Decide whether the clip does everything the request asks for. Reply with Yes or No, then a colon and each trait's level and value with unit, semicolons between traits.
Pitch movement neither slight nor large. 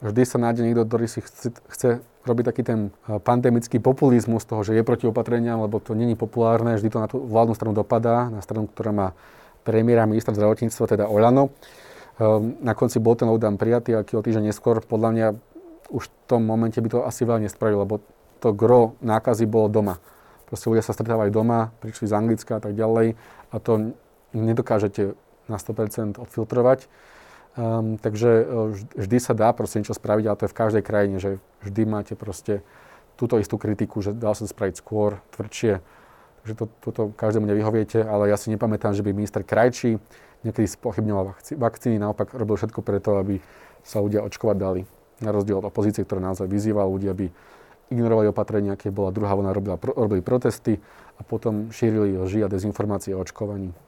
No: narrow, 1.9 semitones